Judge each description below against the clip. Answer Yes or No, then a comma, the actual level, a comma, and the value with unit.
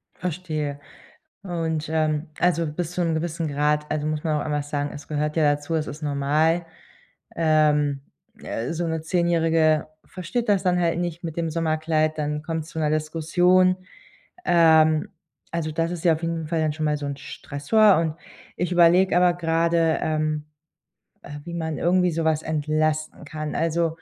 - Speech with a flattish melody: Yes, narrow, 1.8 semitones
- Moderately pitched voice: Yes, medium, 160 Hz